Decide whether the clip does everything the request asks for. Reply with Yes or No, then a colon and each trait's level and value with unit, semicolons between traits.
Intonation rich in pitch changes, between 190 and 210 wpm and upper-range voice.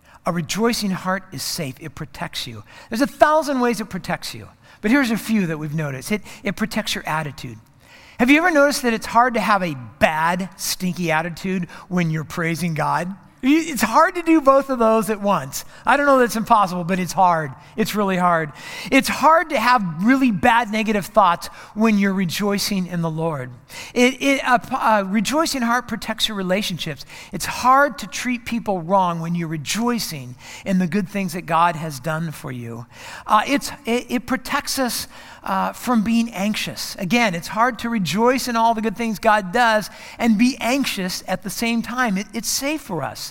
Yes: wide, 5.7 semitones; average, 195 wpm; high, 205 Hz